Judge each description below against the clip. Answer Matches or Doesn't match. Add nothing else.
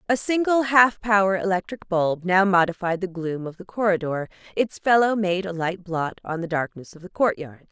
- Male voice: Doesn't match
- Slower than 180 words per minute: Doesn't match